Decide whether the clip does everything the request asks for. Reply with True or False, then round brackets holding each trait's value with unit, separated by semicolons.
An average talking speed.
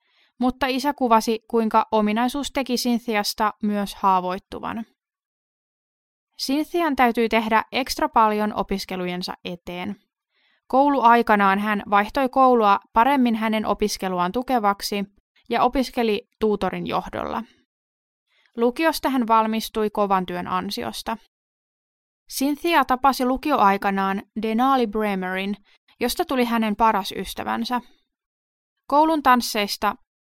False (90 wpm)